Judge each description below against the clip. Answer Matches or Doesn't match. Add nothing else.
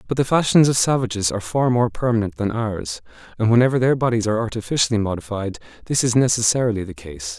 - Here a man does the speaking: Matches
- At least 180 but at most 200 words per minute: Matches